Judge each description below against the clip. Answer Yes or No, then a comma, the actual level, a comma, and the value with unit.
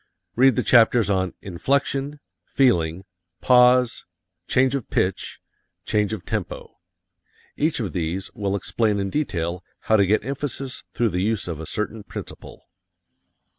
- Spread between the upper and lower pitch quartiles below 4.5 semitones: No, average, 5.2 semitones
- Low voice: Yes, low, 110 Hz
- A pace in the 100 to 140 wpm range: Yes, slow, 135 wpm